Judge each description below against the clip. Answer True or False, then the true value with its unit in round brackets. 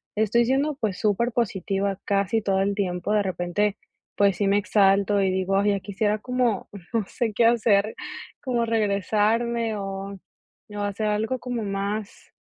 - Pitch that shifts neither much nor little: False (2.3 semitones)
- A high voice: True (205 Hz)